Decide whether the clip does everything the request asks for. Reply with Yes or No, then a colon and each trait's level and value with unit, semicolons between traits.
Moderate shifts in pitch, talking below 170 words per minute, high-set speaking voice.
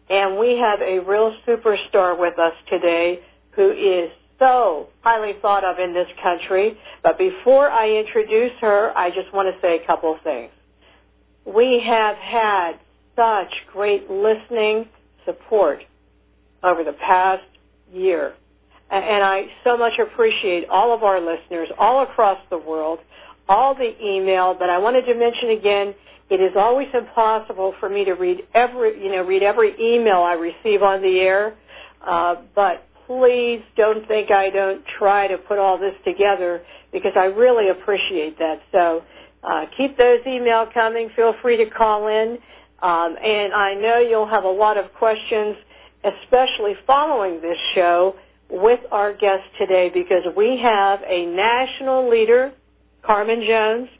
Yes: average, 3.8 semitones; average, 155 wpm; high, 205 Hz